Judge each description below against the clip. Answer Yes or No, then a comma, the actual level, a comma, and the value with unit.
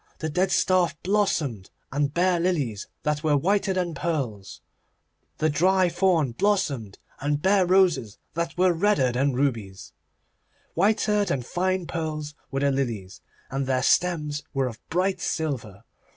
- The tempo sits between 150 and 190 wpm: No, average, 140 wpm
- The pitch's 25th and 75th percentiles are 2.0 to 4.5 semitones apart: No, wide, 5.5 semitones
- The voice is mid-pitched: Yes, medium, 155 Hz